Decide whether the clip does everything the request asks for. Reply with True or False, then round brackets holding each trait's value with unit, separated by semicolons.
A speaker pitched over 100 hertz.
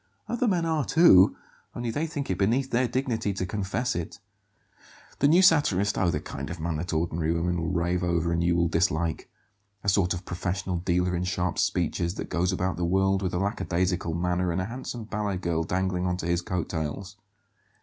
False (90 Hz)